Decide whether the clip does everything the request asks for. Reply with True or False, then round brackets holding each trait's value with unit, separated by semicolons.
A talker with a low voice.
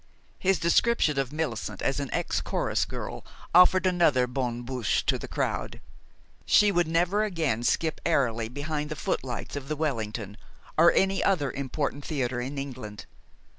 False (145 Hz)